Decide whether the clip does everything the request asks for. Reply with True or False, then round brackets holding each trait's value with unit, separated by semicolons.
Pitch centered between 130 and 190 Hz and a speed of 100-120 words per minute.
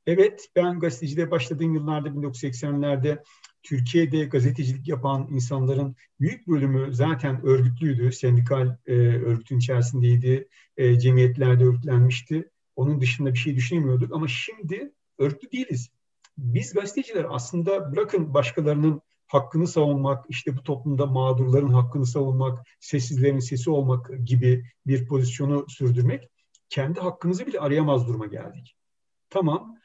True (140 Hz; 115 wpm)